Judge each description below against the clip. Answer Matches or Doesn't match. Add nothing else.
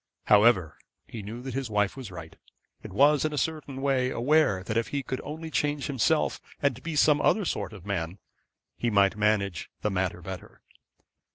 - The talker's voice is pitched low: Matches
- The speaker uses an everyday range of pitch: Doesn't match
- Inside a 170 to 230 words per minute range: Matches